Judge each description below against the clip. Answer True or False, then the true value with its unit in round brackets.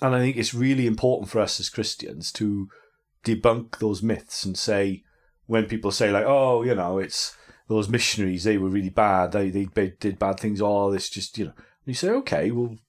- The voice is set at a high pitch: False (110 Hz)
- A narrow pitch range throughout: False (3.2 semitones)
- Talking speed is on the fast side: True (220 wpm)